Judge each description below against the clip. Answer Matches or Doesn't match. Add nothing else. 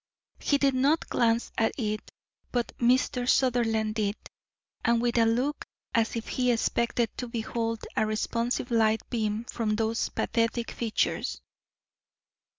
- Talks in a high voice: Matches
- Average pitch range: Doesn't match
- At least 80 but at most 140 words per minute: Matches